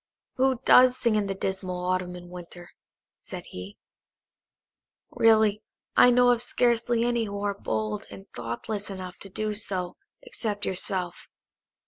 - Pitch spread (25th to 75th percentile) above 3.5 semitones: Yes, average, 4.3 semitones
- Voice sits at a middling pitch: No, high, 200 Hz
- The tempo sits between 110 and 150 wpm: Yes, average, 140 wpm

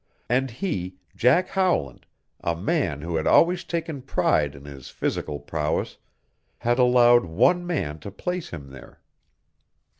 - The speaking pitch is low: Yes, low, 115 Hz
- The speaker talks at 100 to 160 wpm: Yes, average, 140 wpm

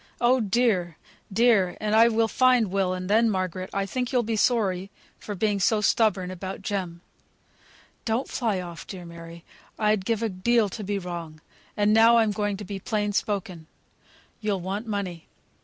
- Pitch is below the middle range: No, high, 205 Hz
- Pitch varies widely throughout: No, average, 3.3 semitones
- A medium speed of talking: Yes, average, 175 wpm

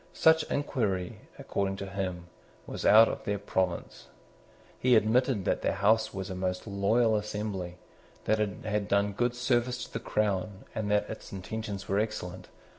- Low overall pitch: Yes, low, 105 Hz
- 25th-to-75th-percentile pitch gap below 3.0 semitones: Yes, narrow, 2.5 semitones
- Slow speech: No, average, 165 wpm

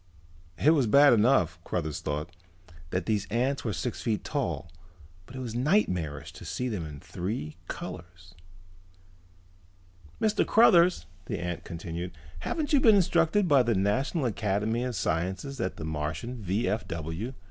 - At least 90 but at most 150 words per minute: Yes, average, 145 wpm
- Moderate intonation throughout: No, wide, 7.9 semitones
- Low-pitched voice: Yes, low, 110 Hz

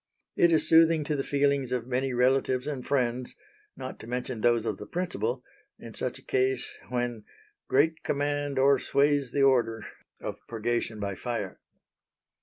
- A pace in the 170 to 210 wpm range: No, average, 155 wpm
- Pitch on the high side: No, low, 130 Hz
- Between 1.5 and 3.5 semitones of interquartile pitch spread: Yes, average, 2.9 semitones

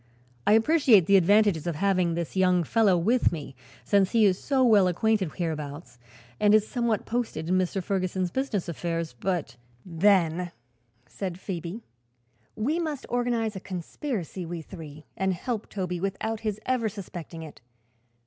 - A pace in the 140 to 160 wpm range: Yes, average, 155 wpm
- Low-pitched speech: No, high, 190 Hz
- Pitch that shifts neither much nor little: Yes, average, 4.4 semitones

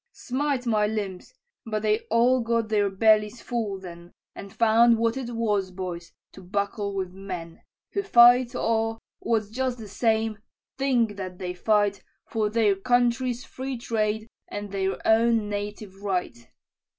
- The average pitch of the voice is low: No, high, 215 Hz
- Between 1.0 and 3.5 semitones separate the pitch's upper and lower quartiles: Yes, average, 2.9 semitones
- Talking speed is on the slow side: No, average, 150 wpm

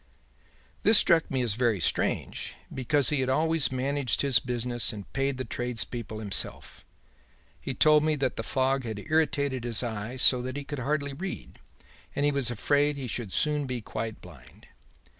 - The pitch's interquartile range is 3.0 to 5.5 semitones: Yes, average, 3.4 semitones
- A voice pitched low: Yes, low, 130 Hz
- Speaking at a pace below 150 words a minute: No, average, 175 wpm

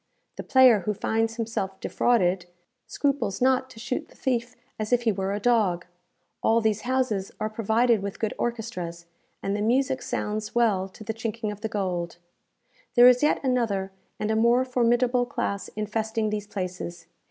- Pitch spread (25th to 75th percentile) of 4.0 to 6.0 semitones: No, average, 3.3 semitones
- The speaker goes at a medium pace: Yes, average, 170 wpm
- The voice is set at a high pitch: Yes, high, 220 Hz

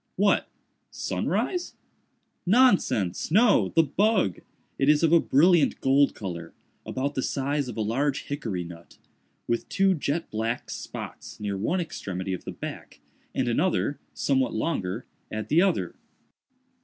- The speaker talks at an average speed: No, slow, 125 wpm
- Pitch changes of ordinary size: No, wide, 7.6 semitones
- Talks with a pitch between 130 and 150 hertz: Yes, low, 135 Hz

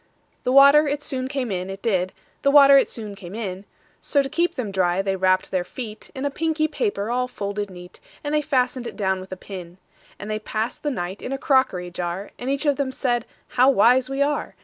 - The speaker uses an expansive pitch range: Yes, wide, 6.3 semitones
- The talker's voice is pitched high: Yes, high, 240 Hz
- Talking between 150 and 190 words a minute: No, fast, 205 wpm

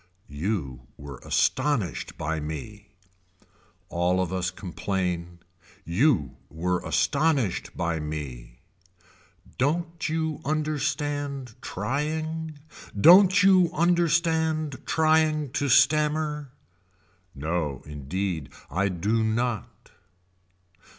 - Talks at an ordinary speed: No, slow, 85 wpm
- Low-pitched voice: Yes, low, 125 Hz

